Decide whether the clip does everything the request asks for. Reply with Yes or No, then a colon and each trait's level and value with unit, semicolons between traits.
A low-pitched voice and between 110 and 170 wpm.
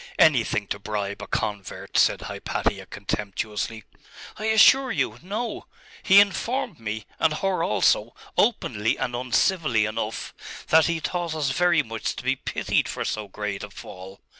Yes: low, 120 Hz; average, 150 wpm